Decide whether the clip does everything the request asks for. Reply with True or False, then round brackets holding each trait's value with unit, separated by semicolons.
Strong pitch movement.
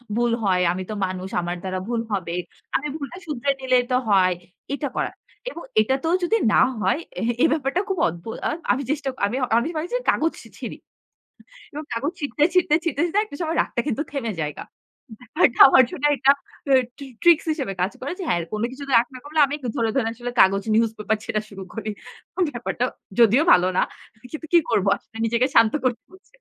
True (5.8 semitones)